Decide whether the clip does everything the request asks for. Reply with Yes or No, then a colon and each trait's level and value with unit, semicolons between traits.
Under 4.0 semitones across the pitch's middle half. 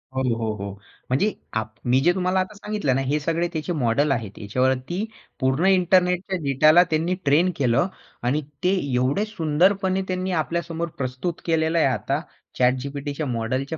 No: wide, 5.6 semitones